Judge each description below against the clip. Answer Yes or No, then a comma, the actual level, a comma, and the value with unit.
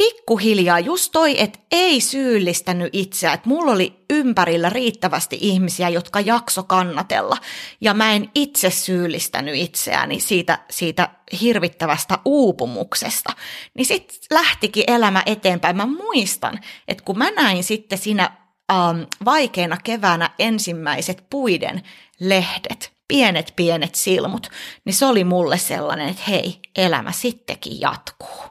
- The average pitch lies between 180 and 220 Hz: Yes, high, 190 Hz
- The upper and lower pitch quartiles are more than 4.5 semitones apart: Yes, average, 5.0 semitones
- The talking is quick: No, average, 125 wpm